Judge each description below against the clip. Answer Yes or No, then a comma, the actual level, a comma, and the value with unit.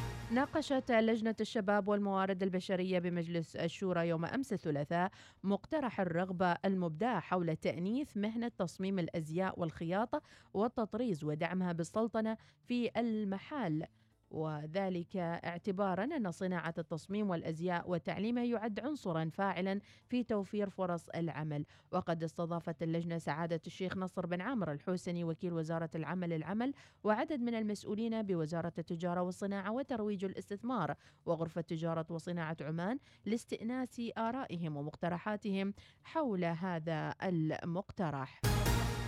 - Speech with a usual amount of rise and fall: Yes, average, 4.2 semitones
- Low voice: No, medium, 185 Hz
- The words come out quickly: No, average, 105 wpm